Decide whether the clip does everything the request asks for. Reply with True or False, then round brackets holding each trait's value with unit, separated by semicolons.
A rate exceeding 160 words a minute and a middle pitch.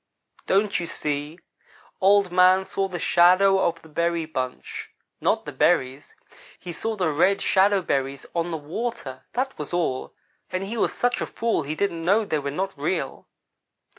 True (170 wpm; 175 Hz)